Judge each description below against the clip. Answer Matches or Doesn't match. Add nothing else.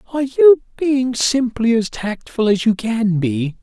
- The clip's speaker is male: Matches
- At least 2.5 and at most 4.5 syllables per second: Matches